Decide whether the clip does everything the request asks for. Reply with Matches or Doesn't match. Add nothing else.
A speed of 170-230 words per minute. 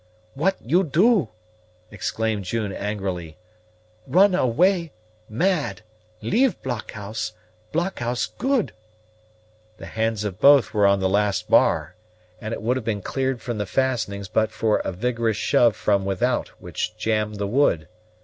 Doesn't match